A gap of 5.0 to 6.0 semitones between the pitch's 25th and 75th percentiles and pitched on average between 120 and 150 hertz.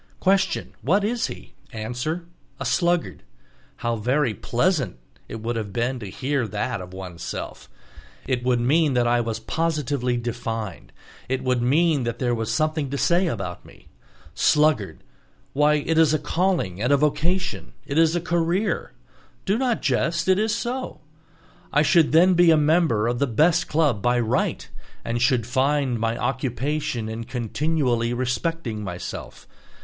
Yes: wide, 5.6 semitones; low, 135 Hz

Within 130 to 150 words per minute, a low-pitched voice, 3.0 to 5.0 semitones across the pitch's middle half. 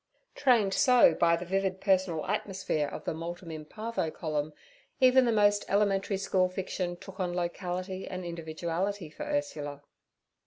No: average, 145 wpm; medium, 185 Hz; average, 3.3 semitones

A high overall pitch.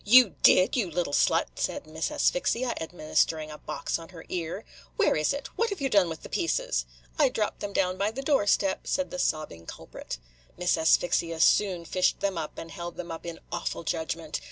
No: medium, 180 Hz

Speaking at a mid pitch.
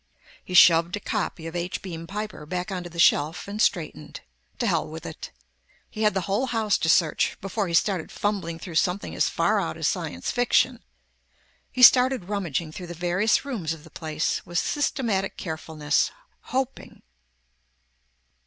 Yes: medium, 180 Hz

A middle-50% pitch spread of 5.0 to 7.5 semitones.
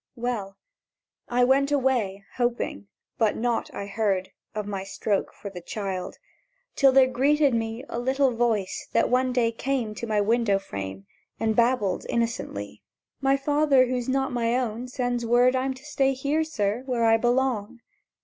No: average, 3.7 semitones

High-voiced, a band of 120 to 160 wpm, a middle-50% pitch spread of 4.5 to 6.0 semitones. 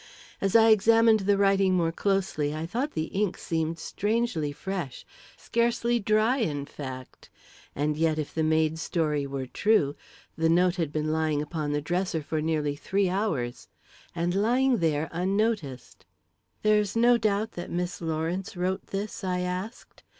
No: medium, 175 Hz; average, 155 wpm; average, 4.9 semitones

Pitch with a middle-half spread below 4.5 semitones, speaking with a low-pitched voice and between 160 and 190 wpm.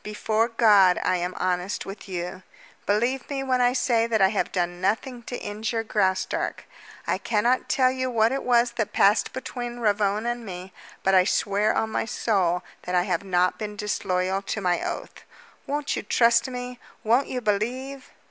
No: average, 4.1 semitones; high, 215 Hz; average, 180 wpm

